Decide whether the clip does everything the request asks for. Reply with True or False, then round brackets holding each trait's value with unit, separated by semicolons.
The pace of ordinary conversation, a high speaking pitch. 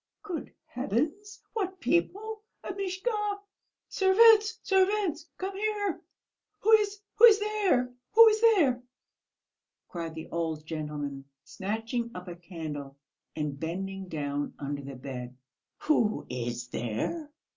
False (110 wpm; 250 Hz)